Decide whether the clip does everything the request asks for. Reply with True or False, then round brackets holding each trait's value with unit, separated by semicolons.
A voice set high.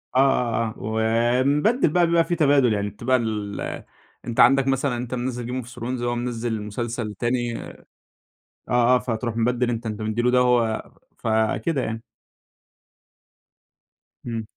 False (120 Hz)